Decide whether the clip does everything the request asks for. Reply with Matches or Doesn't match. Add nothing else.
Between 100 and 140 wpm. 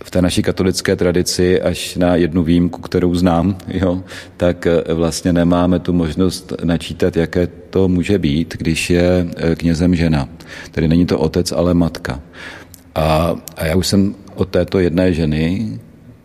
Doesn't match